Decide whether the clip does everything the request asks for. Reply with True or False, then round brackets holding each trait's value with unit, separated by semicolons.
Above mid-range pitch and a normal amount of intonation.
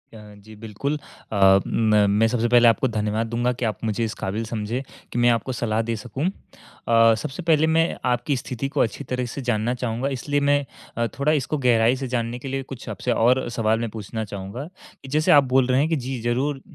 False (120 Hz; 3.2 semitones)